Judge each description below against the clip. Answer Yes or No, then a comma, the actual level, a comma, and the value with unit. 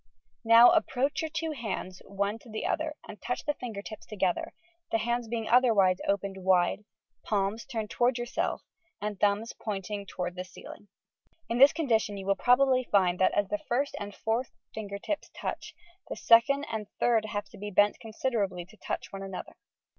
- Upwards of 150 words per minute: Yes, average, 185 wpm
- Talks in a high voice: Yes, high, 215 Hz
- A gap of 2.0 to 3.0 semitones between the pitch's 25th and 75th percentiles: No, average, 3.4 semitones